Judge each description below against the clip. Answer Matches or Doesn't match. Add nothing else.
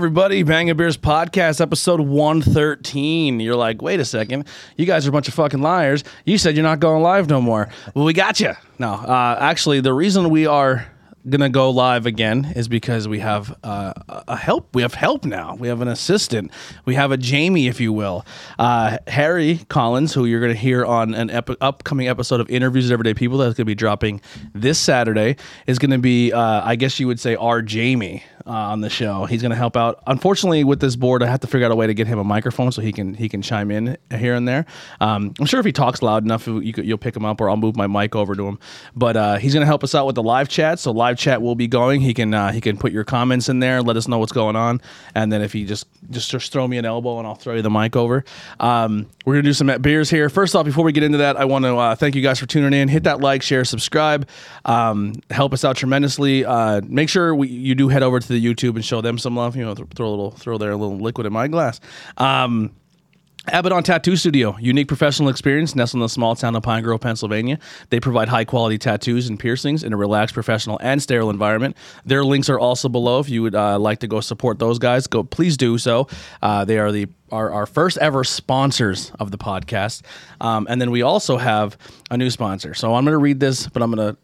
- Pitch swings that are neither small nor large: Matches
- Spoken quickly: Matches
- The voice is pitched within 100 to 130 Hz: Matches